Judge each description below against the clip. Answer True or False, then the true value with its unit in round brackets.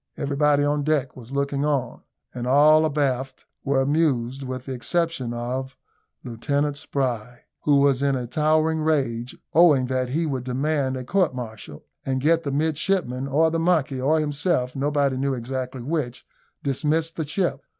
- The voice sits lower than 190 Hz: True (140 Hz)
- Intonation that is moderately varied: True (3.1 semitones)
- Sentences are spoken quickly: False (160 wpm)